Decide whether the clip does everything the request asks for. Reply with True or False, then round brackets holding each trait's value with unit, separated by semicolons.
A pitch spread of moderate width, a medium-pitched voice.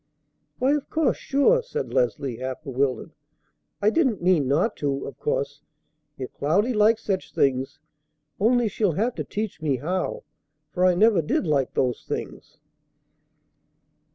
False (8.5 semitones; 180 Hz)